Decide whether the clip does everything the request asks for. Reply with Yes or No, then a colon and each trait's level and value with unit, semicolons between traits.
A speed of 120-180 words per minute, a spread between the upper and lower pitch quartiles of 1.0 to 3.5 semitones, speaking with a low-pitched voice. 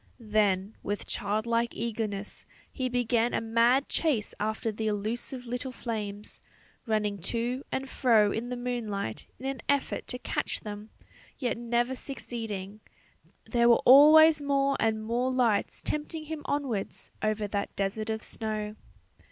No: average, 140 wpm; average, 3.1 semitones; high, 230 Hz